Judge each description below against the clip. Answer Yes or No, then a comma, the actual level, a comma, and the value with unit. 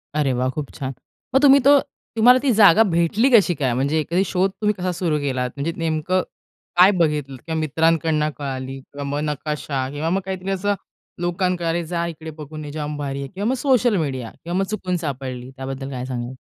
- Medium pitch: Yes, medium, 160 Hz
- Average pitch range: Yes, average, 5.0 semitones